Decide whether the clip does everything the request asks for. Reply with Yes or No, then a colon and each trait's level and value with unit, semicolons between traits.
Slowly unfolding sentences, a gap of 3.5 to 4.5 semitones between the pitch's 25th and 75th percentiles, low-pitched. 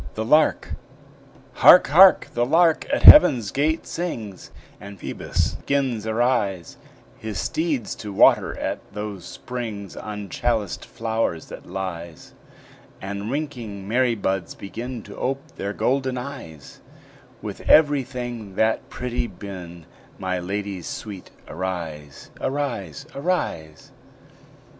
No: slow, 115 wpm; average, 5.2 semitones; low, 110 Hz